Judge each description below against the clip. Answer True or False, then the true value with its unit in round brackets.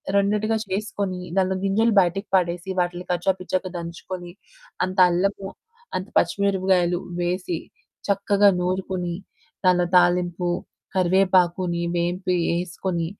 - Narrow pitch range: True (1.7 semitones)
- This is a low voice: False (185 Hz)